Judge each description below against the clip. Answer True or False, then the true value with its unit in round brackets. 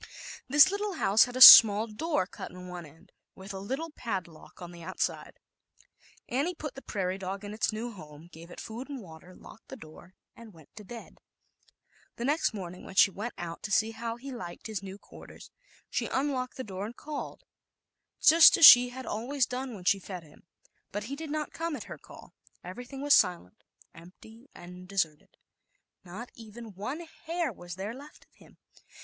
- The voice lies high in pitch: True (215 Hz)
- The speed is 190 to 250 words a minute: True (195 wpm)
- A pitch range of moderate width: False (6.1 semitones)